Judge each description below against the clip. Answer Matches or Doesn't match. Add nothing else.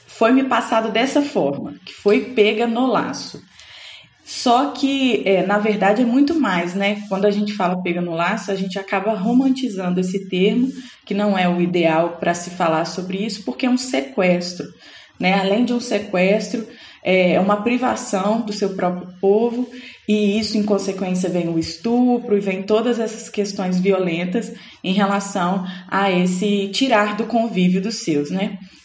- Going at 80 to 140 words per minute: Doesn't match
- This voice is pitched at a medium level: Doesn't match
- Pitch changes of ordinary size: Matches